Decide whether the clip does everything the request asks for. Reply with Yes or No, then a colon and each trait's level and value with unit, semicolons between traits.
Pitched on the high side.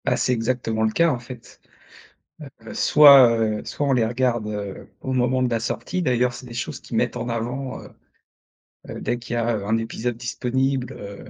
No: low, 120 Hz